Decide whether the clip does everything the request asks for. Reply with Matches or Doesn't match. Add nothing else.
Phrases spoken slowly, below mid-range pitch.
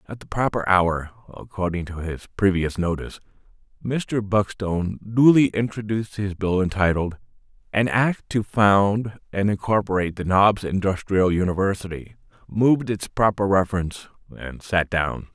Matches